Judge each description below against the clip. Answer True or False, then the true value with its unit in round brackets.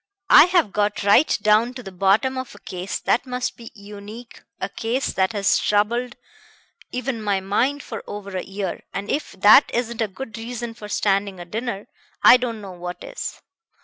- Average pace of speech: True (185 wpm)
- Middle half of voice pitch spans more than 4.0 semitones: False (3.6 semitones)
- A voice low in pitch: False (210 Hz)